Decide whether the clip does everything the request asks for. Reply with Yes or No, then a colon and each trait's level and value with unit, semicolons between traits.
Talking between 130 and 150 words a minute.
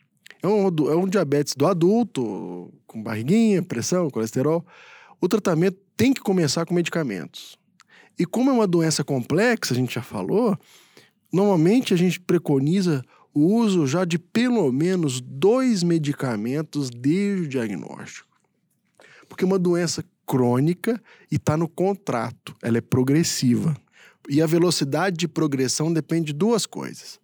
Yes: average, 140 wpm